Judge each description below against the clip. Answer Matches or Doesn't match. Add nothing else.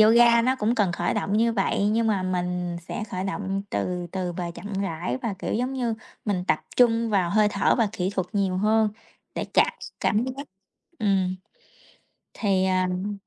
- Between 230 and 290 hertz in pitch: Doesn't match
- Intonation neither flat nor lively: Matches